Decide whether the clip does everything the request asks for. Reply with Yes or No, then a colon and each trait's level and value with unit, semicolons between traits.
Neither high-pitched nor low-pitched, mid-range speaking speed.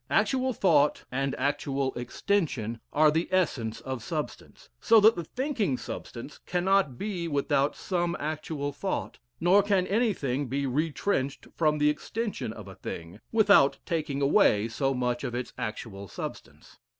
Yes: medium, 150 Hz; average, 145 wpm